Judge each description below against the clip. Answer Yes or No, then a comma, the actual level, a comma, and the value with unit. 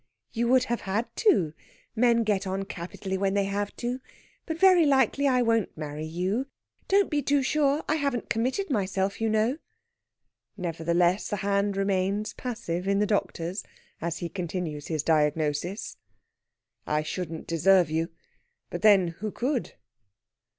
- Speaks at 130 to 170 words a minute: Yes, average, 150 wpm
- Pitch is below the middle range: No, high, 200 Hz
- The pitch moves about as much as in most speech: No, wide, 5.8 semitones